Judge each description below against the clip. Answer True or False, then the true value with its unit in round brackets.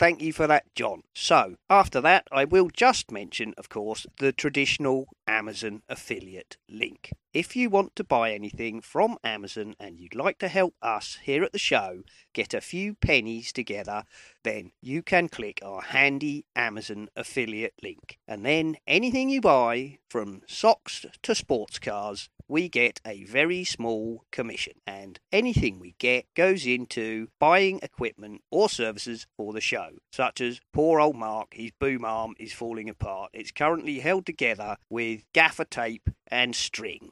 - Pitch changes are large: True (6.5 semitones)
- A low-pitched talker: True (125 Hz)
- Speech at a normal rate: True (160 wpm)